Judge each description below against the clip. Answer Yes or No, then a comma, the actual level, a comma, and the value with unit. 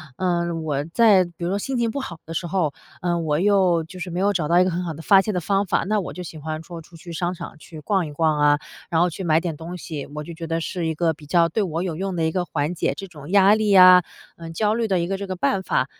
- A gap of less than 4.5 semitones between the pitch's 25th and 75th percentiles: Yes, average, 2.9 semitones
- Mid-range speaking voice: Yes, medium, 175 Hz